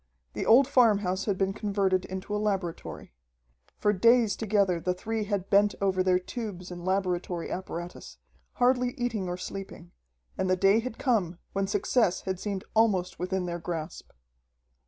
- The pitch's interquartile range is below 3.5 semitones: Yes, average, 2.7 semitones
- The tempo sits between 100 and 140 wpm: No, average, 155 wpm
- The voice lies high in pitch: Yes, high, 195 Hz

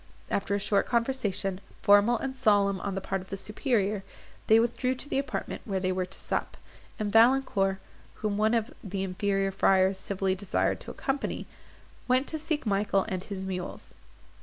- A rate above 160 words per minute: Yes, average, 175 wpm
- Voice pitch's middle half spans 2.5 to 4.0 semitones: Yes, average, 3.3 semitones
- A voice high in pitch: Yes, high, 200 Hz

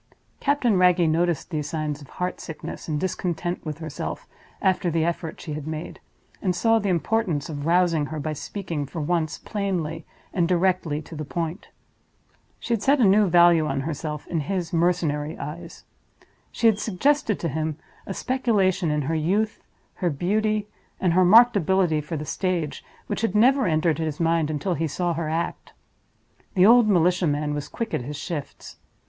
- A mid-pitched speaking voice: Yes, medium, 170 Hz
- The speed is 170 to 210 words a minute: Yes, average, 175 wpm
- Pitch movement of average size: Yes, average, 3.6 semitones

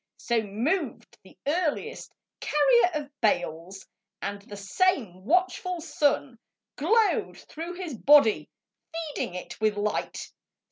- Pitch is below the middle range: No, very high, 285 Hz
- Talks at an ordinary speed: No, slow, 110 wpm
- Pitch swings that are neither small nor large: No, wide, 8.2 semitones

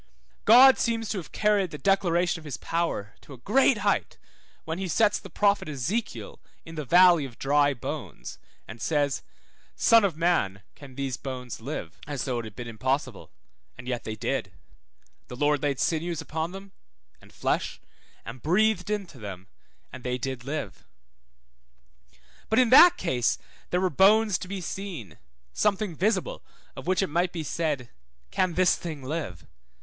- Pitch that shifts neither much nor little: No, wide, 6.9 semitones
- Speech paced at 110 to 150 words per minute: No, average, 165 wpm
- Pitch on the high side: No, medium, 160 Hz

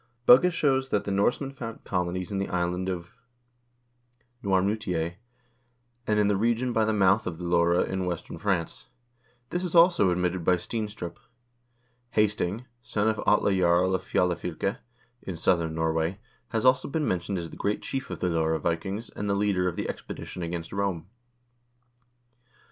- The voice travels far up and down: No, average, 3.7 semitones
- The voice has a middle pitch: No, very low, 95 Hz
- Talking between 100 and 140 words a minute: No, average, 160 wpm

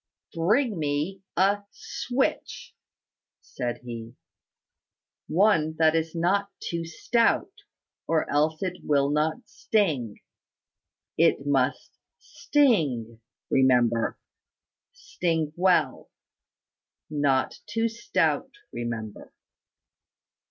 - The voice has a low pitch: No, medium, 160 Hz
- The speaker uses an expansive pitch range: Yes, wide, 6.2 semitones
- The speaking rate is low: Yes, slow, 80 wpm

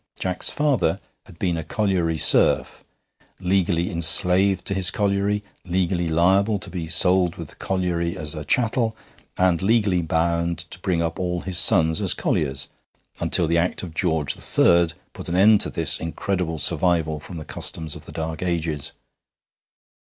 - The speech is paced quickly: No, average, 160 wpm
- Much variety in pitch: No, narrow, 2.6 semitones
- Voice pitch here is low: Yes, very low, 85 Hz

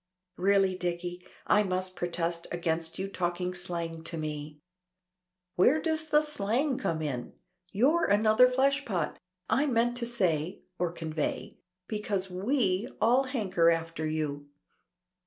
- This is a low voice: No, medium, 185 Hz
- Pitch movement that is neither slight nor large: No, wide, 6.0 semitones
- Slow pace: Yes, slow, 125 wpm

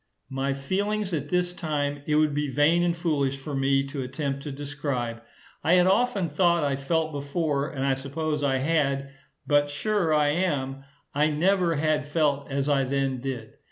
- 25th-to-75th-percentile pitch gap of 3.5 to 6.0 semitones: No, average, 3.0 semitones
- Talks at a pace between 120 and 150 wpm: No, average, 180 wpm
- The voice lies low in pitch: No, medium, 145 Hz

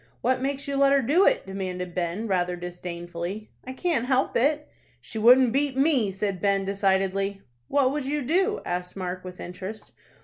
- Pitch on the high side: Yes, high, 210 Hz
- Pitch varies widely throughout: Yes, wide, 6.9 semitones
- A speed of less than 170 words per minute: No, average, 175 wpm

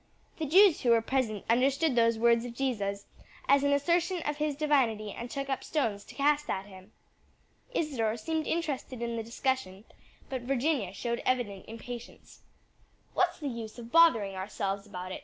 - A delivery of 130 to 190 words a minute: Yes, average, 170 wpm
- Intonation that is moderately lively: Yes, average, 4.8 semitones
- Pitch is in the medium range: No, high, 245 Hz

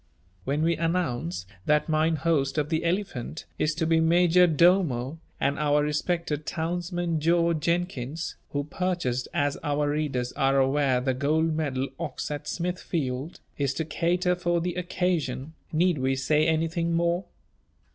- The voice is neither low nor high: Yes, medium, 160 Hz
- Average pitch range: Yes, average, 3.2 semitones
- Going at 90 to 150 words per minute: Yes, average, 145 wpm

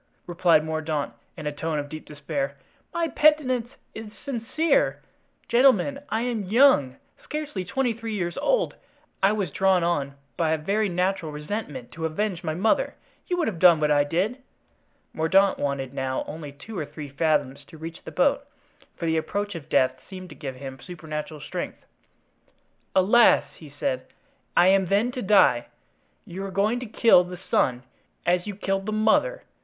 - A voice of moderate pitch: Yes, medium, 180 Hz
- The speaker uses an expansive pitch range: Yes, wide, 6.1 semitones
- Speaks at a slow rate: No, average, 170 wpm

